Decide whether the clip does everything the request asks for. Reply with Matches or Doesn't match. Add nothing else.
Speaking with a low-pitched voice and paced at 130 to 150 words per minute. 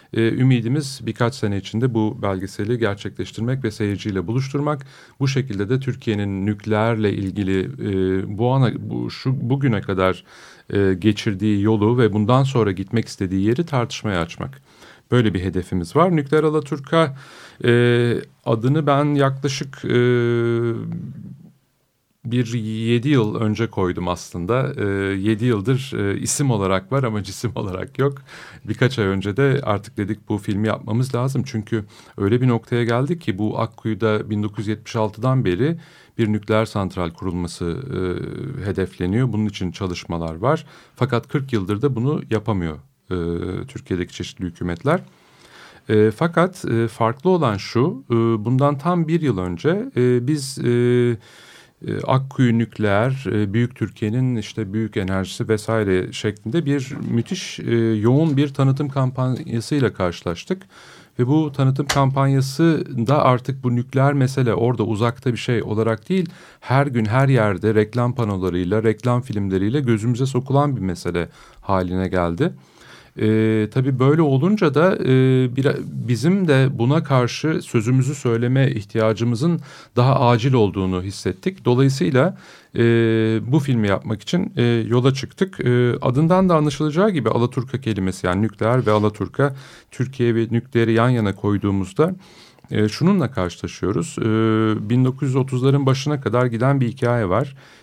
Matches